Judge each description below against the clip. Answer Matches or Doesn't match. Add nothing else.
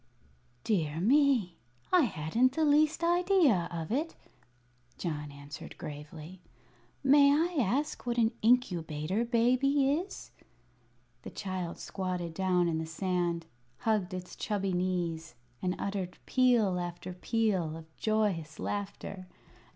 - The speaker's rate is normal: Doesn't match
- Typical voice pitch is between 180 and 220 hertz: Matches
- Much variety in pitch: Matches